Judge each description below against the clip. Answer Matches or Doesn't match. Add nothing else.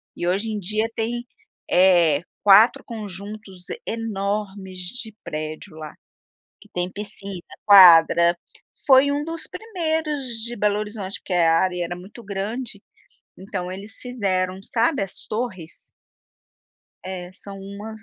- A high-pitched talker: Matches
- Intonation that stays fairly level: Doesn't match